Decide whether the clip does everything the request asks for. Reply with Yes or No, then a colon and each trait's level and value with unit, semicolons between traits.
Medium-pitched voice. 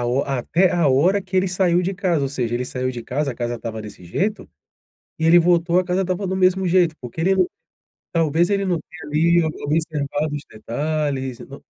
Yes: medium, 160 Hz